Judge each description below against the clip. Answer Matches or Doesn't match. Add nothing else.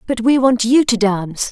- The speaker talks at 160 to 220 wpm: Doesn't match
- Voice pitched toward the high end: Matches